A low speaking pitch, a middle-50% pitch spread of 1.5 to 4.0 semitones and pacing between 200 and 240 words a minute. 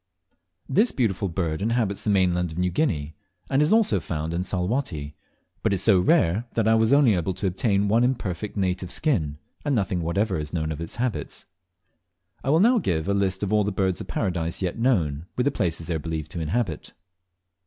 No: very low, 95 Hz; average, 5.3 semitones; fast, 205 wpm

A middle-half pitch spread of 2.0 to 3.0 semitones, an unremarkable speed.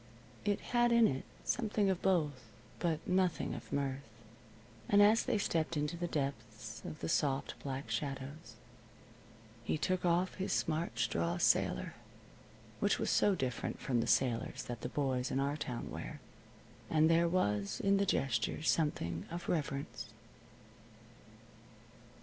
No: average, 5.2 semitones; average, 145 wpm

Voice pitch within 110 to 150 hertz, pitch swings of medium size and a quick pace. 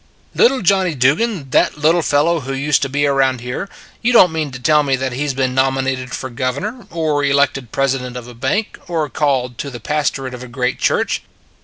Yes: medium, 140 Hz; average, 3.3 semitones; fast, 220 wpm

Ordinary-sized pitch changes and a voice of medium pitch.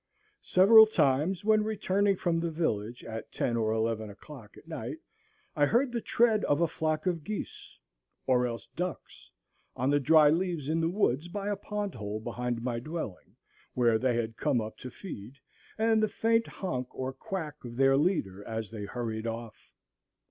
No: wide, 8.2 semitones; medium, 145 Hz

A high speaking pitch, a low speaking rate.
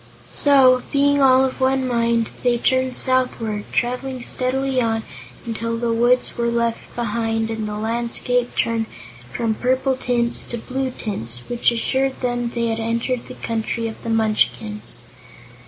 No: high, 235 Hz; average, 150 wpm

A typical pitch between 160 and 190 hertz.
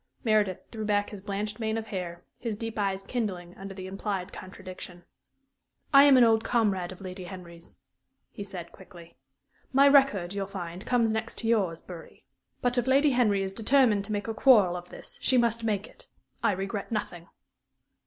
No: high, 205 Hz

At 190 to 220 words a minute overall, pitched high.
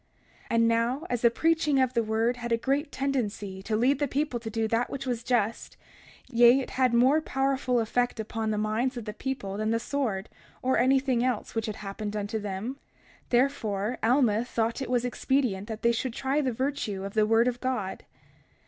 Yes: average, 200 wpm; high, 235 Hz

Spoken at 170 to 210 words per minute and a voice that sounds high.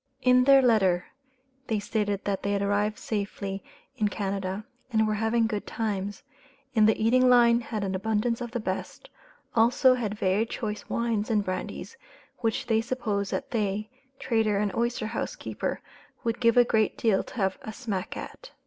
Yes: average, 175 wpm; high, 220 Hz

